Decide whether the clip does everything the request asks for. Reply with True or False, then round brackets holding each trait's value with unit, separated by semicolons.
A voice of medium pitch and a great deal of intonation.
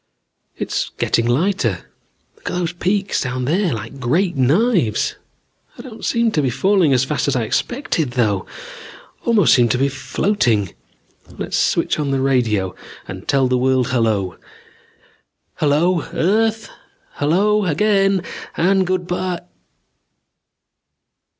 True (150 Hz; 7.3 semitones)